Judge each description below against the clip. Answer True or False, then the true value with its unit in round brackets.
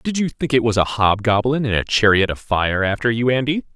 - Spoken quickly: True (255 wpm)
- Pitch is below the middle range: True (115 Hz)